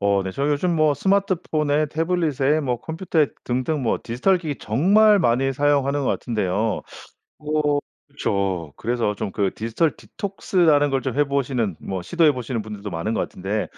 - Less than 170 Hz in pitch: Yes, medium, 140 Hz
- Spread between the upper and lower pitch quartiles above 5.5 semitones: Yes, wide, 6.0 semitones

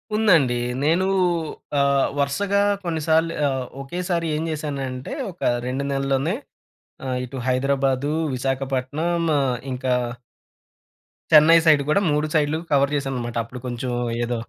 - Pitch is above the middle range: No, medium, 140 Hz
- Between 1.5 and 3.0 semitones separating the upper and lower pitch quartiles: No, average, 3.4 semitones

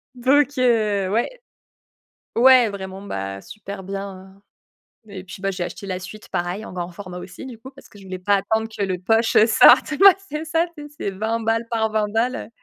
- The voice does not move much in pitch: No, average, 3.5 semitones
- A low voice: No, high, 210 Hz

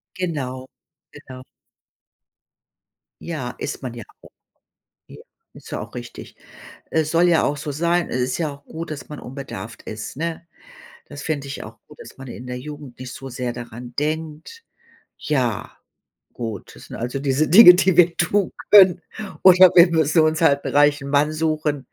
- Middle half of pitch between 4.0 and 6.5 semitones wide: Yes, average, 4.3 semitones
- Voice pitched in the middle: Yes, medium, 145 Hz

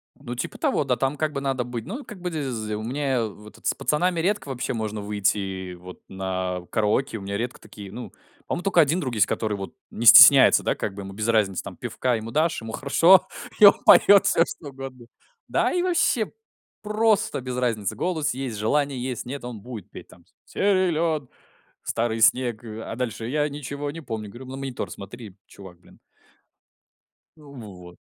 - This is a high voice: No, low, 125 Hz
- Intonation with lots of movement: Yes, wide, 5.7 semitones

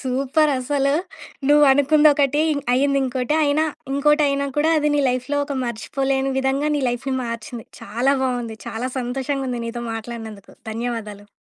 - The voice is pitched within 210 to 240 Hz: No, very high, 265 Hz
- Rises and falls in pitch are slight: No, average, 3.0 semitones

